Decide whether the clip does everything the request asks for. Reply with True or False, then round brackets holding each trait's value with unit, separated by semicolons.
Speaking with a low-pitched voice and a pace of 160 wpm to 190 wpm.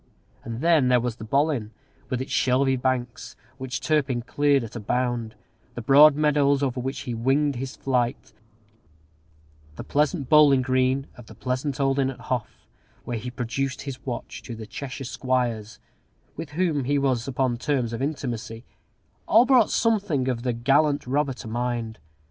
True (130 Hz; 165 wpm)